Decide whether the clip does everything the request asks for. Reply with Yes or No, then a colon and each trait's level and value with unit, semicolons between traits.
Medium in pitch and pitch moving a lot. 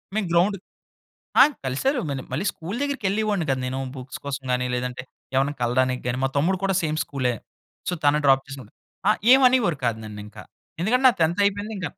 Yes: medium, 150 Hz; wide, 7.7 semitones